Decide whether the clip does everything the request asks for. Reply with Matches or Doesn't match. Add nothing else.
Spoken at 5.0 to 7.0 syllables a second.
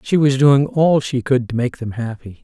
Doesn't match